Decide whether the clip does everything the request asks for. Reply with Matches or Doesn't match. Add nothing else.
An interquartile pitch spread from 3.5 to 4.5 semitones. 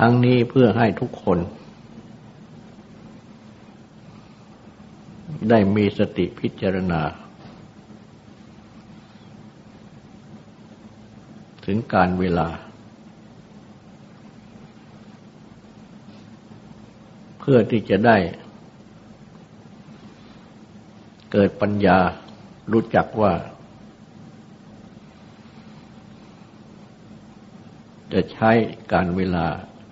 Matches